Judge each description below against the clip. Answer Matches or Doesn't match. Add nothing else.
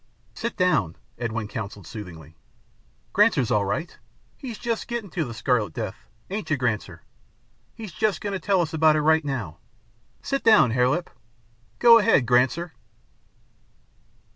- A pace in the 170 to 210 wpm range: Doesn't match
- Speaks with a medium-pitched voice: Matches